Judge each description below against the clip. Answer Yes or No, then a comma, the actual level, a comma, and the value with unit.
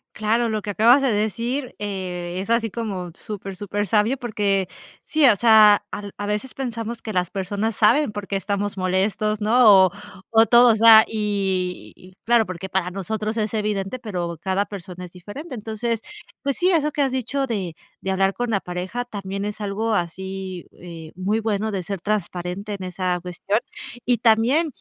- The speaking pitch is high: Yes, high, 210 Hz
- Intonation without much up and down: No, average, 3.1 semitones